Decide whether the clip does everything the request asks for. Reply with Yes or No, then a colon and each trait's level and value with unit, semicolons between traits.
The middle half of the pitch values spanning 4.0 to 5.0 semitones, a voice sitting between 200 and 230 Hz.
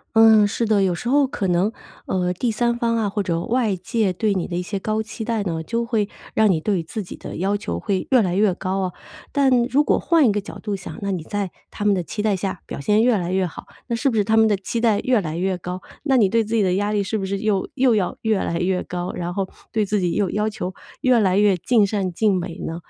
No: average, 3.2 semitones; high, 205 Hz